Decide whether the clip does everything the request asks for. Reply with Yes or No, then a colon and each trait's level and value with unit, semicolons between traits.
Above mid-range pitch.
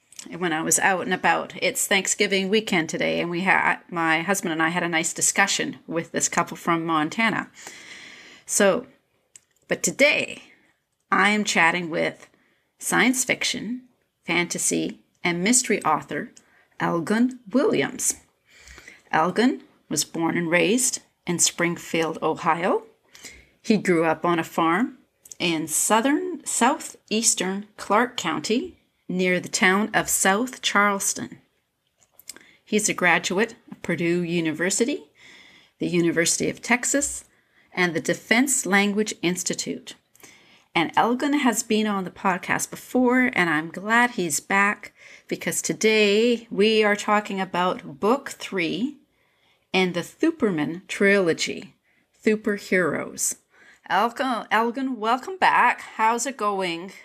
Yes: high, 200 Hz